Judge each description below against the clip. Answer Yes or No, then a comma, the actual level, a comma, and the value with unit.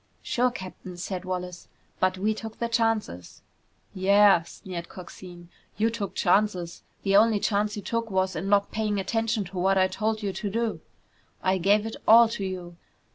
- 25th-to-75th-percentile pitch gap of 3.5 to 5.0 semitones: No, average, 2.8 semitones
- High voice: Yes, high, 200 Hz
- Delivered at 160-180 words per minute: Yes, average, 175 wpm